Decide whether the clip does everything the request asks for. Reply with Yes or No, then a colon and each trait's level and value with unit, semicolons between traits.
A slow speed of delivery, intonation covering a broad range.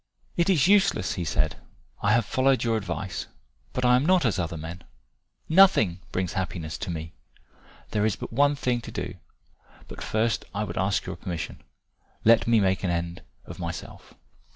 No: average, 175 wpm; wide, 6.1 semitones